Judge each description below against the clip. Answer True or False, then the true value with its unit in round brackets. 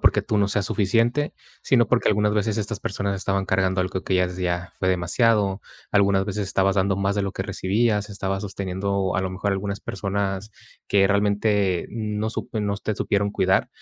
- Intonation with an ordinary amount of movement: False (1.6 semitones)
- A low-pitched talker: True (100 Hz)